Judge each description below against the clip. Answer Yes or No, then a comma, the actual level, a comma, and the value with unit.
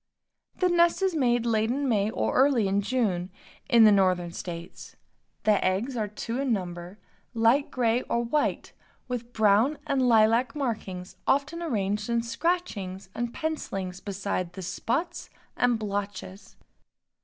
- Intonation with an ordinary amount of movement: Yes, average, 4.7 semitones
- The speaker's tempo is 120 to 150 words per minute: Yes, average, 145 wpm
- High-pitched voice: Yes, high, 225 Hz